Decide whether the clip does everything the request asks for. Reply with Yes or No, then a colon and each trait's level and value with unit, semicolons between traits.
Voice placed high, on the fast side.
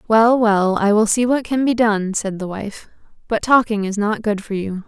Yes: high, 215 Hz; fast, 235 wpm